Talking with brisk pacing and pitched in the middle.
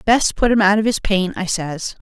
No: fast, 260 wpm; high, 200 Hz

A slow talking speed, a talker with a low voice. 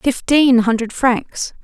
No: slow, 110 wpm; high, 245 Hz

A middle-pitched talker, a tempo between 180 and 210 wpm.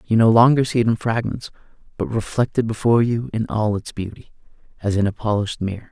No: low, 110 Hz; fast, 205 wpm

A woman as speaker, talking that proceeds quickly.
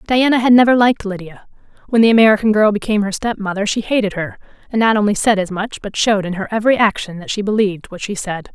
Yes: female; fast, 230 wpm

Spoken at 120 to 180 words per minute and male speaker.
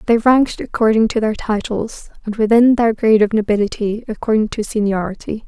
No: average, 165 wpm; female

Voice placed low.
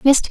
No: very high, 270 Hz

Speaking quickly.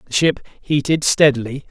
No: average, 140 wpm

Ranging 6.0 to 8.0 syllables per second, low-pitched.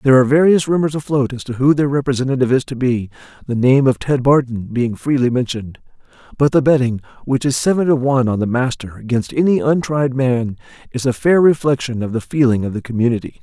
Yes: 6.2 syllables/s; low, 130 Hz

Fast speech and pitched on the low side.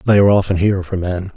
Yes: fast, 265 wpm; very low, 95 Hz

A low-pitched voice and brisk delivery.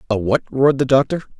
Yes: low, 130 Hz; fast, 215 wpm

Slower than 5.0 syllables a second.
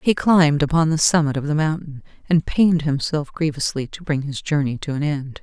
No: 5.5 syllables/s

